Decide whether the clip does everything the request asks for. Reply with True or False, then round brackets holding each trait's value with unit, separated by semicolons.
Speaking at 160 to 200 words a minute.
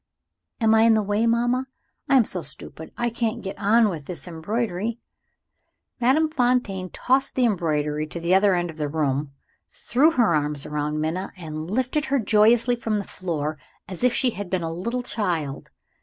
True (185 wpm)